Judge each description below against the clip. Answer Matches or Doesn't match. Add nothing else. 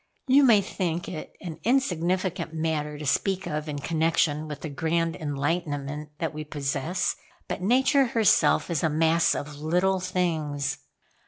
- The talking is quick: Doesn't match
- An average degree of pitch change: Matches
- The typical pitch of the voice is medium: Matches